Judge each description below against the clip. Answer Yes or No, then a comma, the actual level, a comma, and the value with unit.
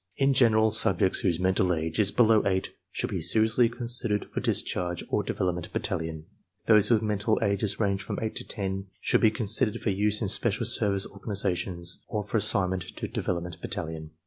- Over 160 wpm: Yes, average, 180 wpm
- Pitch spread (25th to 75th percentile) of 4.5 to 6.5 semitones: No, average, 3.2 semitones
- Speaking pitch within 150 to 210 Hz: No, low, 100 Hz